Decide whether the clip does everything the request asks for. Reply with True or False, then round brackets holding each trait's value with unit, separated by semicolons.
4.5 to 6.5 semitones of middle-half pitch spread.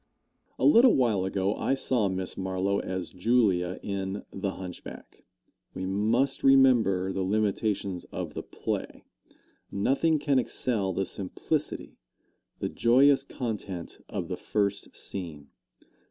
True (4.8 semitones)